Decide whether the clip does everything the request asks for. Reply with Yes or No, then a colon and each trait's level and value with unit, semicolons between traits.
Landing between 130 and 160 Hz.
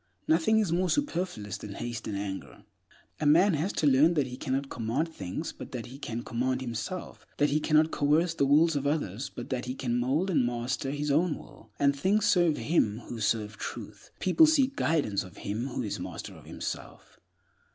Yes: medium, 140 Hz